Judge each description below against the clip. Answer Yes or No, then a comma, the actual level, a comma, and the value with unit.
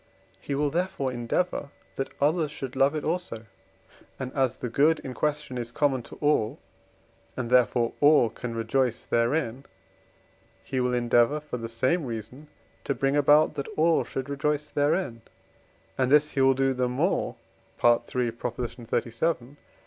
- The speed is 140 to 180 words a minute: Yes, average, 150 wpm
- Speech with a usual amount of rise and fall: Yes, average, 3.7 semitones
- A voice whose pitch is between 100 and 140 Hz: Yes, low, 135 Hz